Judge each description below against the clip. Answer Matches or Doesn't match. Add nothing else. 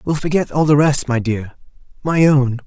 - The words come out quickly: Doesn't match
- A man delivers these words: Matches